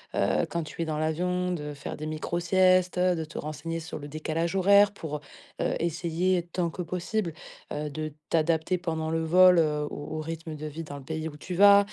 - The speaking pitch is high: No, medium, 165 Hz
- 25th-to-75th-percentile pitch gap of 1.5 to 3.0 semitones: Yes, narrow, 2.6 semitones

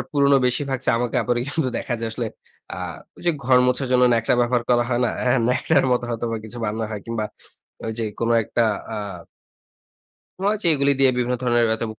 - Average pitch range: No, narrow, 2.1 semitones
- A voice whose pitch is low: Yes, low, 125 Hz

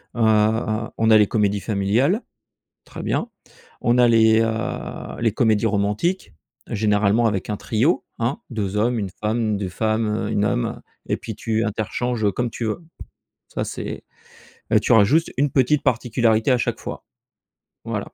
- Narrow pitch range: Yes, narrow, 2.2 semitones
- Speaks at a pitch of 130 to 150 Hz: No, low, 110 Hz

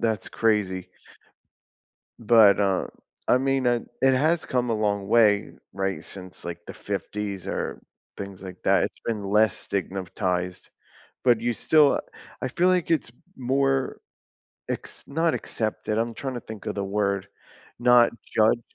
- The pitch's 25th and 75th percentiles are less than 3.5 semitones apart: No, average, 4.0 semitones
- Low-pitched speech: Yes, low, 110 Hz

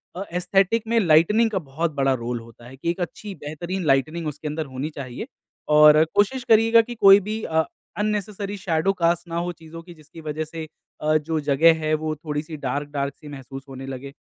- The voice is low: No, medium, 160 Hz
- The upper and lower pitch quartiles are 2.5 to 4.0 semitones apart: No, average, 4.6 semitones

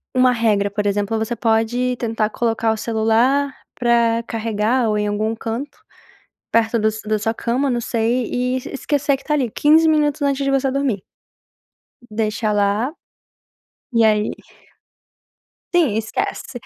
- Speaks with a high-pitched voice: Yes, high, 230 Hz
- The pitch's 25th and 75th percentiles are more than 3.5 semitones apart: No, average, 3.1 semitones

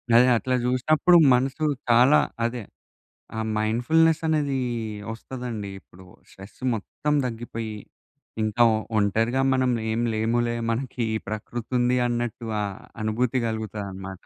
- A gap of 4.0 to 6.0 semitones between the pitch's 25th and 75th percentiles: No, average, 2.7 semitones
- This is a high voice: No, low, 120 Hz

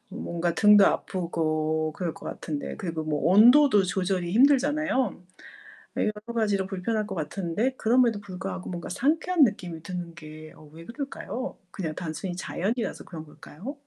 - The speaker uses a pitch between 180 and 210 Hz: Yes, high, 190 Hz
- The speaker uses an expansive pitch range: Yes, wide, 5.7 semitones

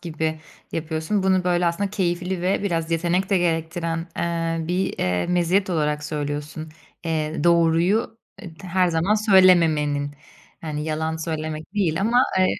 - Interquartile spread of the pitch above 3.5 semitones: No, average, 2.7 semitones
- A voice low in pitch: No, medium, 165 Hz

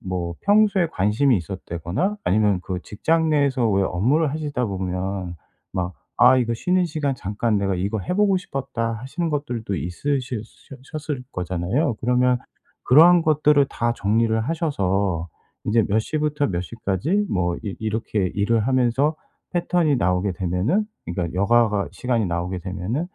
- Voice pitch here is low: Yes, low, 115 Hz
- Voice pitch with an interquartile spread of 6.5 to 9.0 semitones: Yes, wide, 7.5 semitones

